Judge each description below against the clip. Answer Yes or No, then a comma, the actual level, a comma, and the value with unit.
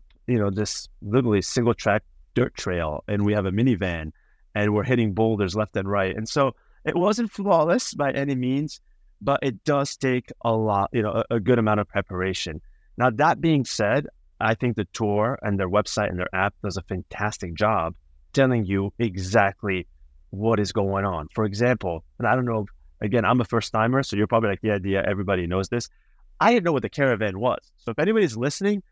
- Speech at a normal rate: No, fast, 210 wpm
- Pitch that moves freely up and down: No, average, 4.1 semitones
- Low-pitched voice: Yes, low, 105 Hz